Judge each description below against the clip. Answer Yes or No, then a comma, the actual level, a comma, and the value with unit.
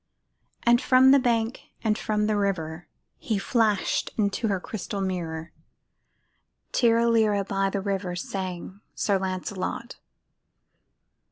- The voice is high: Yes, high, 200 Hz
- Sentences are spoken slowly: Yes, slow, 110 wpm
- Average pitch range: Yes, average, 3.0 semitones